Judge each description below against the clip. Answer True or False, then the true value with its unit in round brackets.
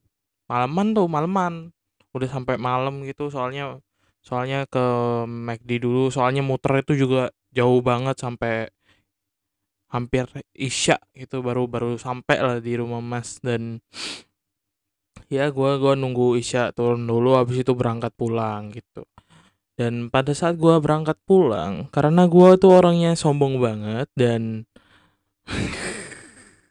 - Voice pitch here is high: False (125 Hz)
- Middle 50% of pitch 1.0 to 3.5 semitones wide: True (2.9 semitones)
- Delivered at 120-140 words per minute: True (125 wpm)